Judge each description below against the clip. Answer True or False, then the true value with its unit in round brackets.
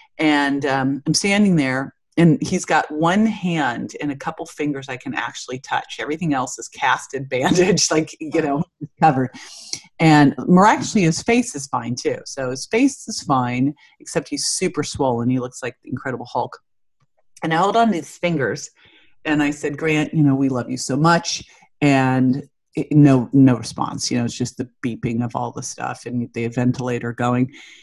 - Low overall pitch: False (145 Hz)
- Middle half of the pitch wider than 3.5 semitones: True (4.4 semitones)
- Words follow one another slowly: False (185 wpm)